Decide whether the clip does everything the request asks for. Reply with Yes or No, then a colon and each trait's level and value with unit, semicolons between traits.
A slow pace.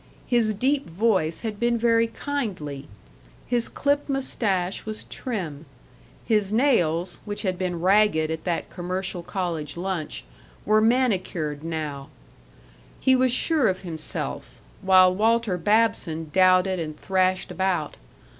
Yes: slow, 125 wpm